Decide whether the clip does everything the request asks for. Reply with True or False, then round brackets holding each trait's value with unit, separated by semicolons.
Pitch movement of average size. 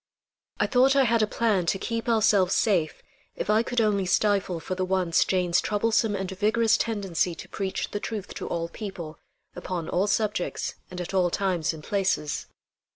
True (3.4 semitones)